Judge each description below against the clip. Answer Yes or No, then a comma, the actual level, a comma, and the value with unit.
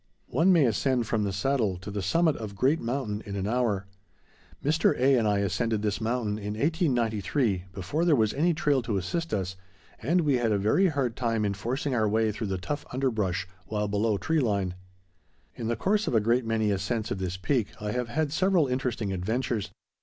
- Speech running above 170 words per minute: Yes, fast, 205 wpm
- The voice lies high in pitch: No, low, 115 Hz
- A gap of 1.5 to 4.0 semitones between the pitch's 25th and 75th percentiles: No, average, 4.8 semitones